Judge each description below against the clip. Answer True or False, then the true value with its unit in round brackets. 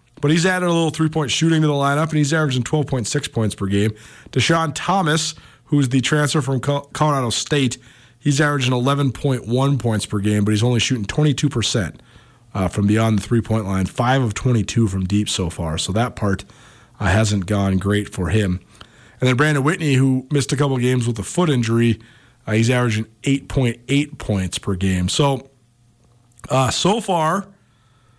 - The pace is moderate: True (180 wpm)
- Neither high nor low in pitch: False (125 Hz)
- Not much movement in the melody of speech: False (4.8 semitones)